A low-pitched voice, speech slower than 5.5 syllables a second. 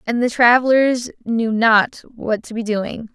No: high, 230 Hz; 4.0 syllables/s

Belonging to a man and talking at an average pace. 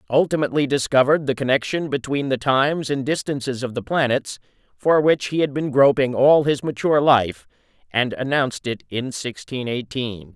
Yes: male; average, 160 wpm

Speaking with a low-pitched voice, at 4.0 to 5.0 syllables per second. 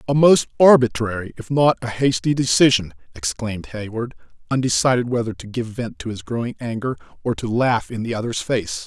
No: low, 115 Hz; 5.5 syllables/s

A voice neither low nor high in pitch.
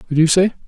Yes: medium, 170 Hz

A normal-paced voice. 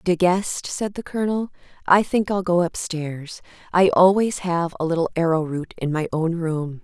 Yes: average, 175 wpm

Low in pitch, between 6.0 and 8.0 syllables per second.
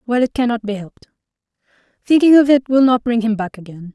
No: high, 235 Hz; 6.4 syllables/s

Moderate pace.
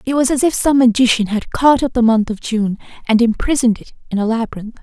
No: fast, 235 wpm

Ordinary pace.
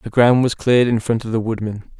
No: fast, 270 wpm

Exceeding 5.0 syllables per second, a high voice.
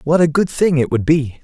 No: 5.3 syllables/s; medium, 150 Hz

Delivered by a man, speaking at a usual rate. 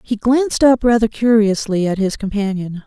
No: female; average, 170 wpm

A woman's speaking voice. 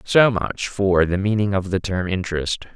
No: male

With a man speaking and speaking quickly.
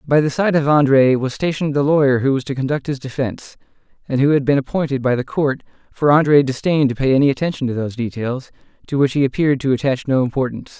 Yes: male; fast, 230 wpm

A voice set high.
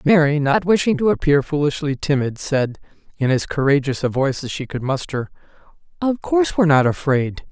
No: medium, 145 Hz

